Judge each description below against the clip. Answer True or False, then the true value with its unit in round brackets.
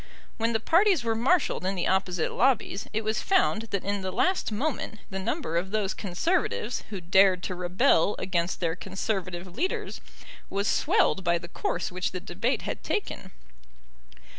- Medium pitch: False (195 Hz)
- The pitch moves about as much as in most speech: True (4.3 semitones)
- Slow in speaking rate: False (165 wpm)